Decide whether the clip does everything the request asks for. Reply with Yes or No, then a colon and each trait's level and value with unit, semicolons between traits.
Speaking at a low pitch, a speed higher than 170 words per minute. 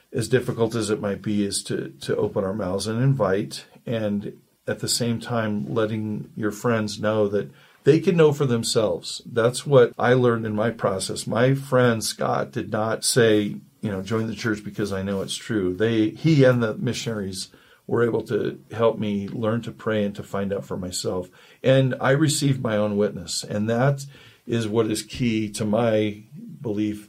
Yes: low, 110 Hz; average, 190 wpm